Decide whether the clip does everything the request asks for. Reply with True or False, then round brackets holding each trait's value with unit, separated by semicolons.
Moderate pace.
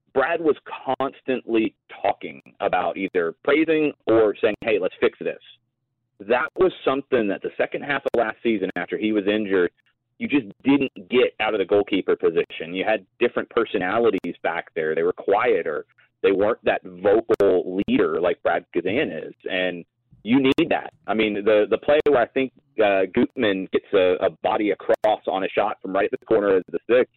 True (185 wpm)